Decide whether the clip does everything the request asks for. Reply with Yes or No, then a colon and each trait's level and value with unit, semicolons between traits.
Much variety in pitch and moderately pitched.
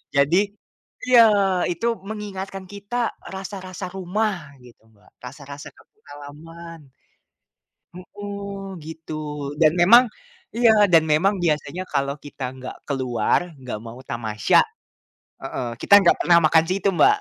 Yes: wide, 5.7 semitones; medium, 170 Hz